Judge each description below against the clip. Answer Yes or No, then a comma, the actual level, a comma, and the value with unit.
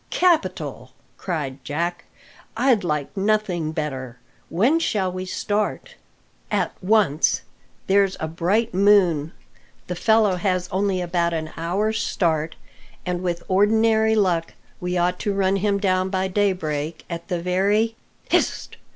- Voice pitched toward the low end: No, medium, 185 Hz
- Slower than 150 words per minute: Yes, slow, 135 wpm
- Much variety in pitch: No, average, 3.4 semitones